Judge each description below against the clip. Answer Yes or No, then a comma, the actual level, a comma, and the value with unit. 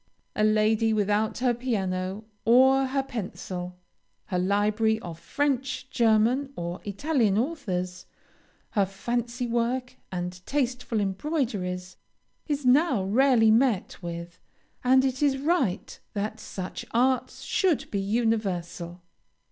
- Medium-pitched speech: No, high, 220 Hz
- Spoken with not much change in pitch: No, average, 5.2 semitones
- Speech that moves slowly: Yes, slow, 115 wpm